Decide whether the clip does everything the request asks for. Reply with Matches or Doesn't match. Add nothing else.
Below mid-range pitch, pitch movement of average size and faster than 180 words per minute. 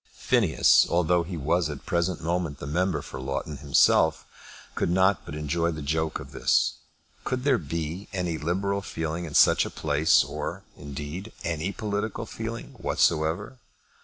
Doesn't match